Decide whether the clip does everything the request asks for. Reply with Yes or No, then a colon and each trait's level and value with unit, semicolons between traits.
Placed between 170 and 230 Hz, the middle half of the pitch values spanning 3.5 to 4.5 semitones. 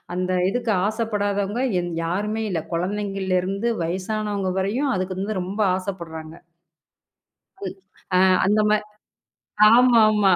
No: high, 200 Hz; narrow, 2.6 semitones